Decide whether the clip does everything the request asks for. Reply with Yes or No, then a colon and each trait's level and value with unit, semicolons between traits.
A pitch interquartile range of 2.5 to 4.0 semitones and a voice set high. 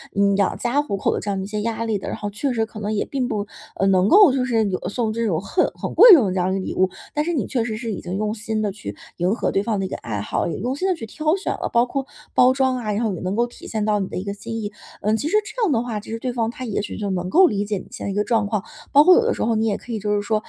Yes: average, 3.6 semitones; high, 220 Hz